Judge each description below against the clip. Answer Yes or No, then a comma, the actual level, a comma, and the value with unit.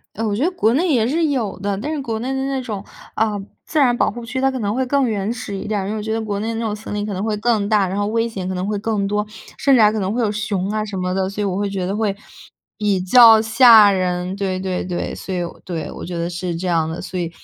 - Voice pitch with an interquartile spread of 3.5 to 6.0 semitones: No, average, 3.0 semitones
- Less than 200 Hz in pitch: No, high, 210 Hz